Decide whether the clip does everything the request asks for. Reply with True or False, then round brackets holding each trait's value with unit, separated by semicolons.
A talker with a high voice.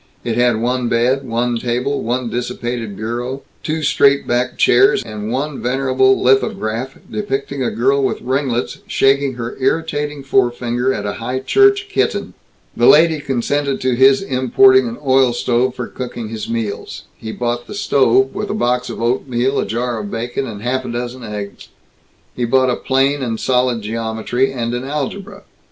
False (125 Hz)